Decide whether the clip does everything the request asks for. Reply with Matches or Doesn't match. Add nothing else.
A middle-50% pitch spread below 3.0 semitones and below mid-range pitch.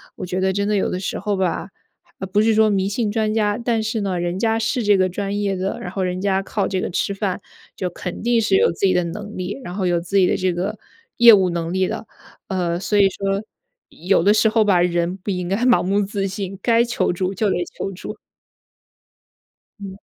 Doesn't match